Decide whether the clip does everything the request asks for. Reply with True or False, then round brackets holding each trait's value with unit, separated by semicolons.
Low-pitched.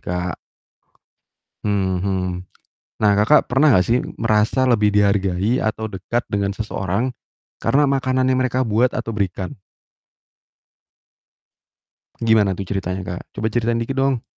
True (105 Hz)